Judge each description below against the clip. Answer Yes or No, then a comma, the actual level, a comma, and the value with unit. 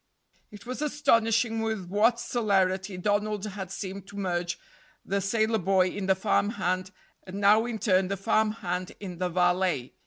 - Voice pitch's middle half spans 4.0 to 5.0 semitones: No, average, 2.8 semitones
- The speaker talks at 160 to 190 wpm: Yes, average, 165 wpm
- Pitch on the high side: Yes, high, 200 Hz